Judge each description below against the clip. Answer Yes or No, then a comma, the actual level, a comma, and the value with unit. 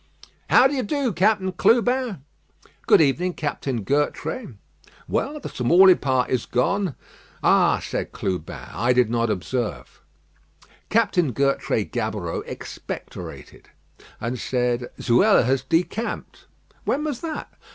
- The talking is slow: Yes, slow, 110 wpm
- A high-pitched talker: No, medium, 150 Hz